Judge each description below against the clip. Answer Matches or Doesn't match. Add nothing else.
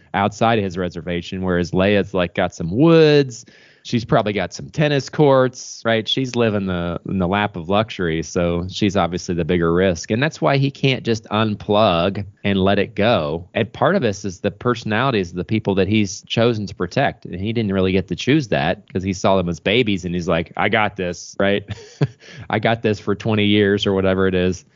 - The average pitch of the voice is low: Matches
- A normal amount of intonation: Matches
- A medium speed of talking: Doesn't match